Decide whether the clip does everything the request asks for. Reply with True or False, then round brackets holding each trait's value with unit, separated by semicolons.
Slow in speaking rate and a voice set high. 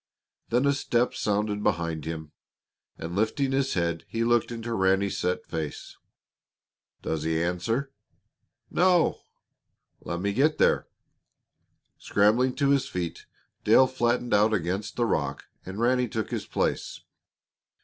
False (130 wpm; 105 Hz)